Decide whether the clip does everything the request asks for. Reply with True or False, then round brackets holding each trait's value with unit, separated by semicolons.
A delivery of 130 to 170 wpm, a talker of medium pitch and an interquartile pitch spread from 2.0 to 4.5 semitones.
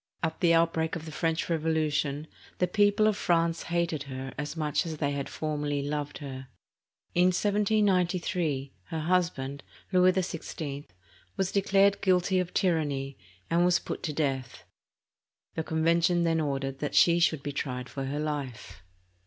True (155 wpm; 160 Hz; 3.6 semitones)